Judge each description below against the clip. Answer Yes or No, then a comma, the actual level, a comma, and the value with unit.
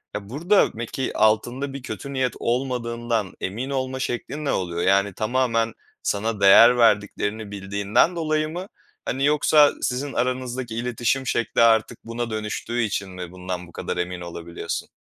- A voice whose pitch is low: Yes, low, 115 Hz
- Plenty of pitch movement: No, average, 4.3 semitones